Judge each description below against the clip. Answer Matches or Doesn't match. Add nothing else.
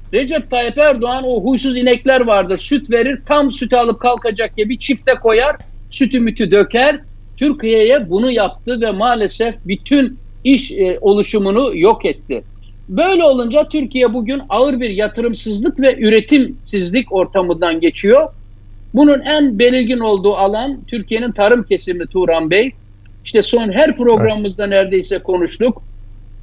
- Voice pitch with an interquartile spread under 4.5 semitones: Doesn't match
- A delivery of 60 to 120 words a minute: Doesn't match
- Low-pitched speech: Doesn't match